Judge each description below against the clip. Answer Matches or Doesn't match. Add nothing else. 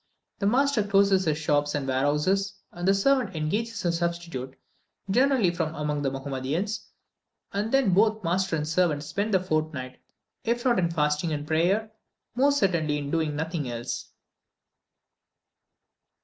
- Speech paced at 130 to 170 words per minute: Matches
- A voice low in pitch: Doesn't match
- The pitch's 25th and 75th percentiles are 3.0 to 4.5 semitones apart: Doesn't match